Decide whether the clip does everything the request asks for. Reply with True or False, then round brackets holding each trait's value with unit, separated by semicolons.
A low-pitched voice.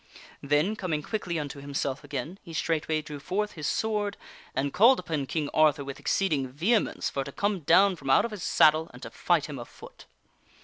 False (155 Hz)